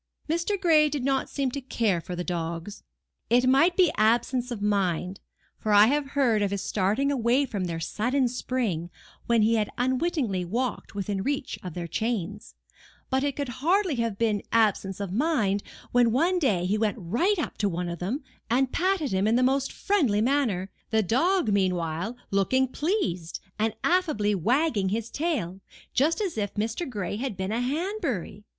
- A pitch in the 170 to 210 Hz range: No, high, 230 Hz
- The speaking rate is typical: Yes, average, 180 wpm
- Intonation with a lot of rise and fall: Yes, wide, 5.9 semitones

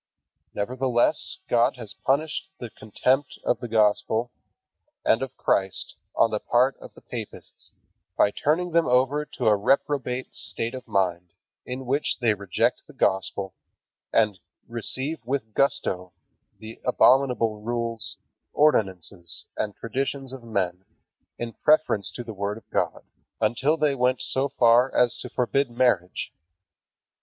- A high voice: No, low, 120 Hz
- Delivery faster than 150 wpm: No, slow, 135 wpm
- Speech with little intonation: No, average, 4.1 semitones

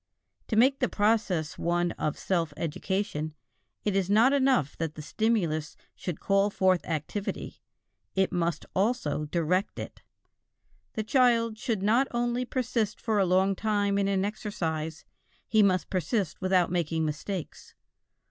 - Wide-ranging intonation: No, average, 4.6 semitones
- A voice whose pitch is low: No, high, 195 Hz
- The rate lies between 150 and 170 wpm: No, average, 140 wpm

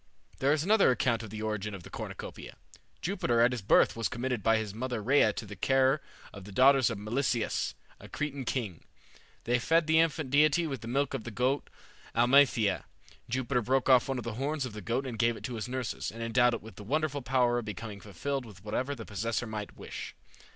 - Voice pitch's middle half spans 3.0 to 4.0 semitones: Yes, average, 3.5 semitones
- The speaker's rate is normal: No, fast, 220 wpm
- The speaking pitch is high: No, low, 120 Hz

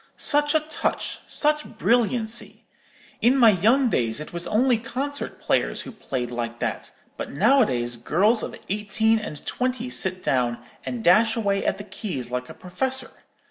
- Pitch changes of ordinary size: No, wide, 7.4 semitones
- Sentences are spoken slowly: No, average, 160 wpm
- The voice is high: Yes, high, 220 Hz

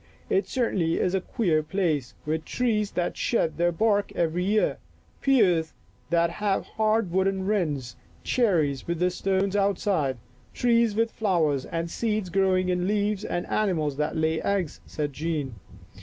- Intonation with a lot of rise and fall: No, average, 4.5 semitones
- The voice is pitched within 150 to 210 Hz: Yes, medium, 185 Hz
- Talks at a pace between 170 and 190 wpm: No, average, 155 wpm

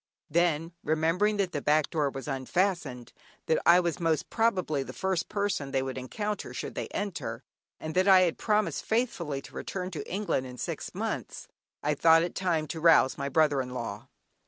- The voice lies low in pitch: No, medium, 165 Hz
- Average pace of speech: Yes, average, 185 wpm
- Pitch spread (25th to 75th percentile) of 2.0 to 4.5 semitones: No, average, 4.9 semitones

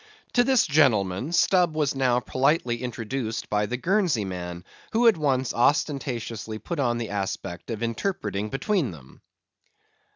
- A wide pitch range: Yes, wide, 6.4 semitones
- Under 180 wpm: Yes, average, 140 wpm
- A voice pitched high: No, low, 125 Hz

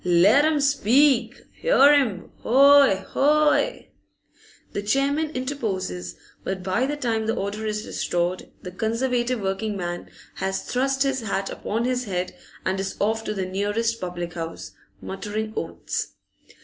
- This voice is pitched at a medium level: No, high, 220 Hz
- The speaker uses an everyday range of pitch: No, wide, 5.8 semitones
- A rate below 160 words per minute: Yes, average, 140 wpm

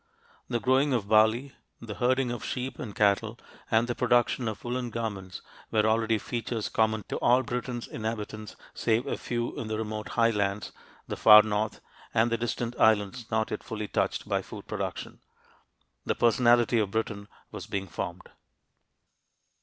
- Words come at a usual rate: Yes, average, 160 wpm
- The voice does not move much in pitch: Yes, narrow, 2.1 semitones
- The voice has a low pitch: Yes, low, 110 Hz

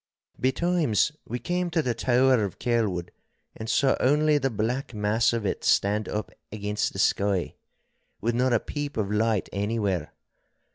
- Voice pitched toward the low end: Yes, low, 115 Hz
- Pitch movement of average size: Yes, average, 4.2 semitones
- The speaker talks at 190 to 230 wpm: No, average, 155 wpm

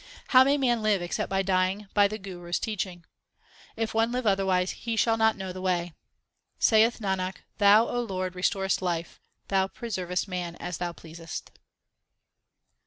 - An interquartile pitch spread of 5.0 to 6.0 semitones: No, average, 3.4 semitones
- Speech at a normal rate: Yes, average, 170 wpm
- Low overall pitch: No, high, 195 Hz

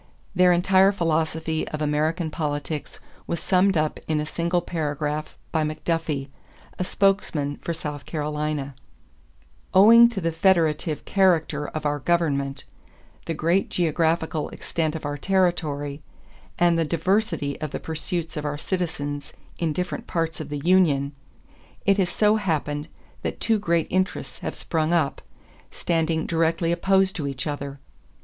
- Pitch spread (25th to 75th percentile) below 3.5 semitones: Yes, average, 2.9 semitones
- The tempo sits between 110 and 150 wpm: Yes, average, 140 wpm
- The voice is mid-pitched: Yes, medium, 160 Hz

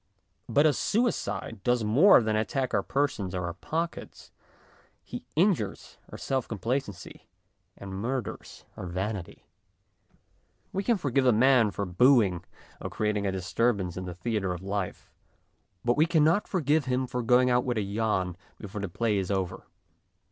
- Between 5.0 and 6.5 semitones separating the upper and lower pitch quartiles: Yes, wide, 5.5 semitones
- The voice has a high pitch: No, low, 110 Hz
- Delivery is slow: No, average, 160 wpm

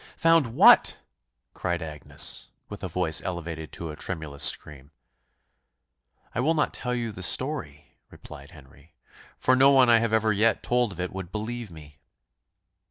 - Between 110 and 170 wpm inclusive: Yes, average, 160 wpm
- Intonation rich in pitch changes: Yes, wide, 7.7 semitones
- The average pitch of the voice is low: Yes, very low, 95 Hz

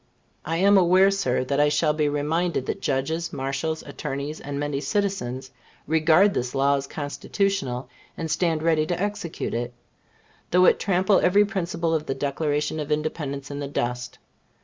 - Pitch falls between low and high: Yes, medium, 155 Hz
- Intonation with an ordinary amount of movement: Yes, average, 3.9 semitones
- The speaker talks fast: No, average, 165 wpm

